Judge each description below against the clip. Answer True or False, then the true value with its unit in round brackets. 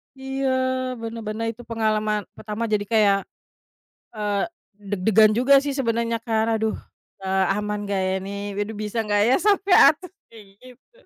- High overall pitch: True (220 Hz)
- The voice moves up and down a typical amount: False (2.1 semitones)